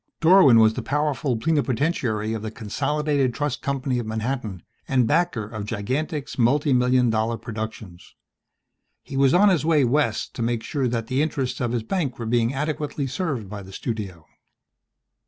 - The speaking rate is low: No, average, 160 wpm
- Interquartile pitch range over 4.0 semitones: Yes, average, 4.6 semitones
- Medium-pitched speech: No, low, 125 Hz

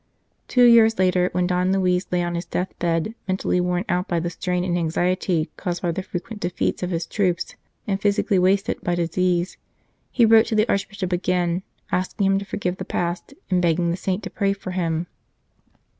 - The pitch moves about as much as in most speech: No, narrow, 1.9 semitones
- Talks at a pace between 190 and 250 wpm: Yes, average, 195 wpm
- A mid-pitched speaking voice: Yes, medium, 180 Hz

